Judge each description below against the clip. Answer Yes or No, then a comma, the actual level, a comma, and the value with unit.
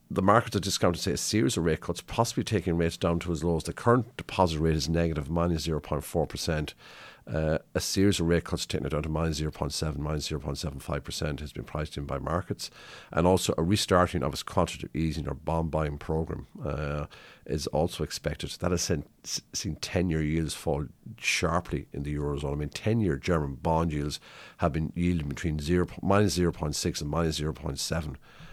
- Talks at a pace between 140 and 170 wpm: No, average, 200 wpm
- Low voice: Yes, very low, 80 Hz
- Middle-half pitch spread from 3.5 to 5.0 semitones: No, average, 2.8 semitones